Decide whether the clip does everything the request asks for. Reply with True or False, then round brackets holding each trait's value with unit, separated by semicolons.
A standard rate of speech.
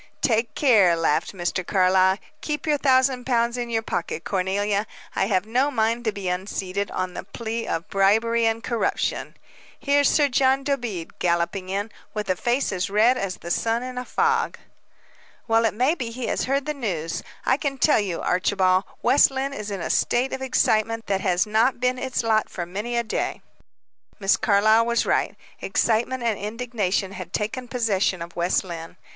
True (185 wpm)